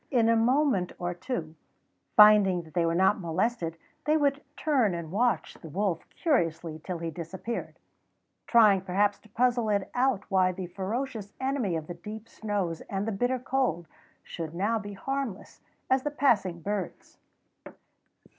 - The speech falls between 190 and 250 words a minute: No, average, 155 wpm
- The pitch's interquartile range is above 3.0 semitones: Yes, wide, 5.6 semitones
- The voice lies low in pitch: No, high, 205 Hz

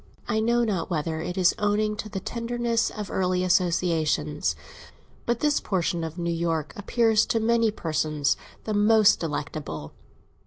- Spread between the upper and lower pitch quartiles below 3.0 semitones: No, average, 5.3 semitones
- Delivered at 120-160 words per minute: Yes, average, 150 wpm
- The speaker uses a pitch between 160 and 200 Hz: Yes, medium, 185 Hz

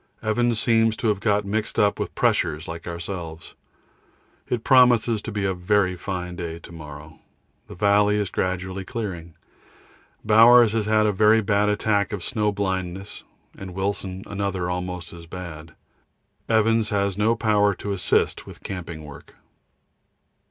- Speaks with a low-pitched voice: Yes, low, 100 Hz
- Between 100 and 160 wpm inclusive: Yes, average, 150 wpm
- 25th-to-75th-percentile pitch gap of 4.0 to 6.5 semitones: No, average, 3.2 semitones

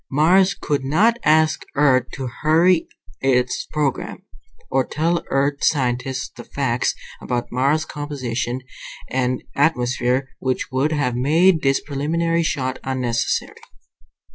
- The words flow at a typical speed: No, slow, 115 wpm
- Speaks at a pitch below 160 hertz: Yes, medium, 140 Hz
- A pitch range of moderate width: Yes, average, 3.5 semitones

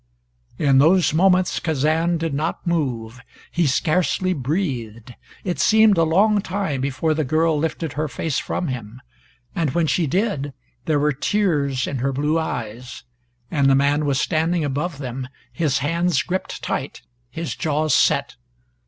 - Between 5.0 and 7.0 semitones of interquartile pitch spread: No, average, 3.9 semitones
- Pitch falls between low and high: Yes, medium, 155 Hz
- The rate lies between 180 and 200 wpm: No, average, 155 wpm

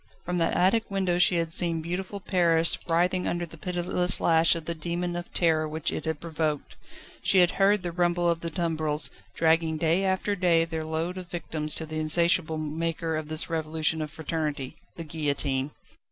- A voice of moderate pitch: Yes, medium, 165 Hz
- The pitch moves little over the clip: Yes, narrow, 1.9 semitones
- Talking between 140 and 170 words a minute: No, average, 185 wpm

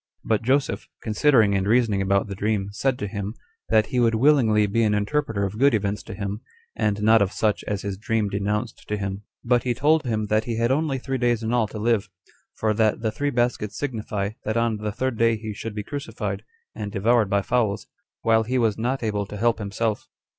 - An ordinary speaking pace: No, fast, 220 wpm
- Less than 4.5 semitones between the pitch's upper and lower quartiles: Yes, narrow, 2.6 semitones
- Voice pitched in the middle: No, low, 110 Hz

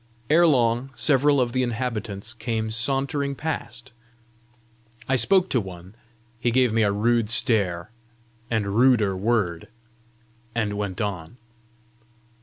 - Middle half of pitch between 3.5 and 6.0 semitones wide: Yes, average, 3.8 semitones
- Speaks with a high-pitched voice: No, low, 115 Hz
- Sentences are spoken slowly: Yes, slow, 120 wpm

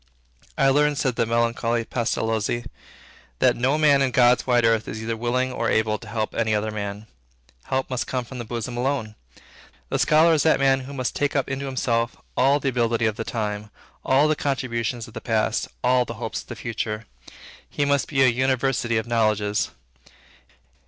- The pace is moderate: Yes, average, 190 wpm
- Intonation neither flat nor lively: Yes, average, 3.0 semitones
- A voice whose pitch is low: Yes, low, 120 Hz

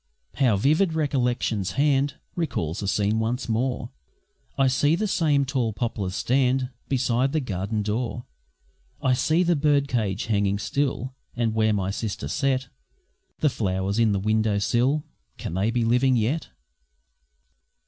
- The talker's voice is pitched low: Yes, low, 120 Hz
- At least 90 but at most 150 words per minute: Yes, average, 145 wpm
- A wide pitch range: No, average, 4.4 semitones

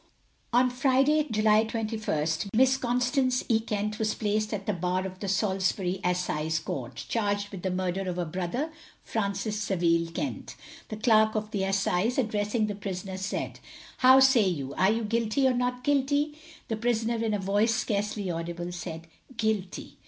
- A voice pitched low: No, high, 210 Hz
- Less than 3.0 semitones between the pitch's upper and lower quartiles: No, average, 3.8 semitones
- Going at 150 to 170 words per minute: Yes, average, 165 wpm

